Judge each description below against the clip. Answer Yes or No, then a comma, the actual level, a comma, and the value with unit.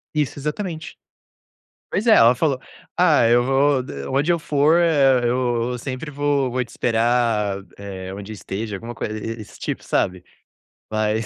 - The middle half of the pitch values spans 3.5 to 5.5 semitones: Yes, average, 5.0 semitones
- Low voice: Yes, low, 125 Hz